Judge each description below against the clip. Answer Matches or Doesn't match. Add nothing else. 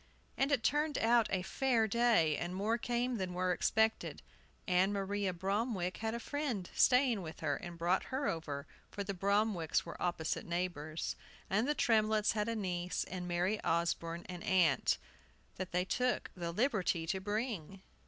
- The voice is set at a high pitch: Matches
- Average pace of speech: Matches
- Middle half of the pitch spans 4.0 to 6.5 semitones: Matches